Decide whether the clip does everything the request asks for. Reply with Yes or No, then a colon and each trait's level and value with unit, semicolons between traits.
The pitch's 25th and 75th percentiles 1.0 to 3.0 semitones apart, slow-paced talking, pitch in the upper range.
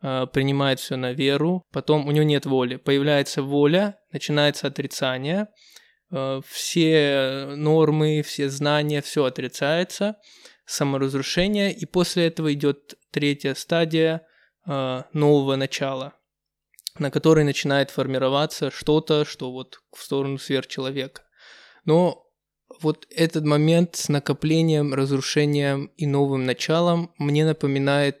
No: average, 2.7 semitones; slow, 105 wpm; medium, 145 Hz